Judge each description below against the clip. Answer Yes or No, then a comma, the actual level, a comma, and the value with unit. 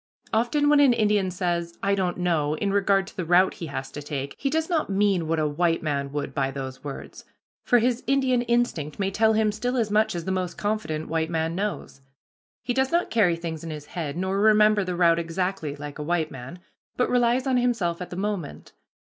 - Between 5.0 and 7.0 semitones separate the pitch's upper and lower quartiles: Yes, wide, 5.4 semitones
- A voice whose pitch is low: No, medium, 185 Hz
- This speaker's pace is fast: Yes, fast, 220 wpm